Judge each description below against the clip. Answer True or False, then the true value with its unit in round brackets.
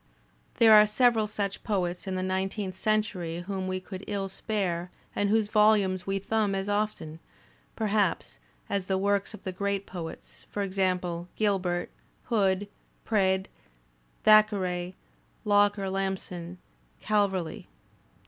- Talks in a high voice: True (195 Hz)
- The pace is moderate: False (130 wpm)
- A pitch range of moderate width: False (2.1 semitones)